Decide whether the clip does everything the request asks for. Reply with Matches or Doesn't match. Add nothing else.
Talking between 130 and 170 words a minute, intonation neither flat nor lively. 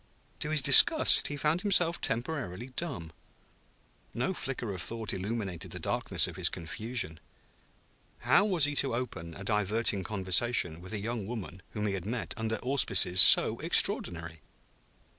Doesn't match